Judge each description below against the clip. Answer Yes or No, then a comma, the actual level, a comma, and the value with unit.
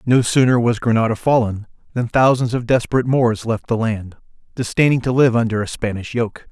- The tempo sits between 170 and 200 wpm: Yes, average, 185 wpm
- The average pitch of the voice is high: No, low, 120 Hz